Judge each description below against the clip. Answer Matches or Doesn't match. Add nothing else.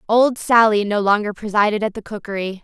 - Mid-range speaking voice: Doesn't match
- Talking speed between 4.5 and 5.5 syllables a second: Doesn't match